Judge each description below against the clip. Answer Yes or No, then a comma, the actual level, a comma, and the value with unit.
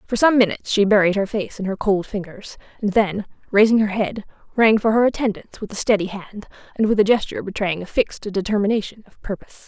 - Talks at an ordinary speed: No, fast, 210 wpm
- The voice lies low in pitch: No, high, 205 Hz